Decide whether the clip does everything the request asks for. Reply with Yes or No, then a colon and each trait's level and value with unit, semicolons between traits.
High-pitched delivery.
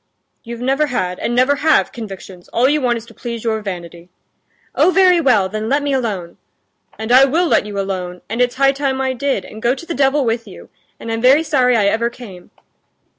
Yes: high, 240 Hz